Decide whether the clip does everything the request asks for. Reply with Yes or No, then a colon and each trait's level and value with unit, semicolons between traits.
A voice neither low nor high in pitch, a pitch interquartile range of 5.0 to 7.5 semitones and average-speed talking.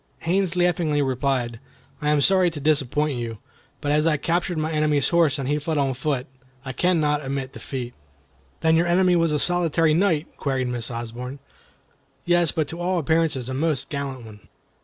No: medium, 150 Hz; average, 3.9 semitones; average, 180 wpm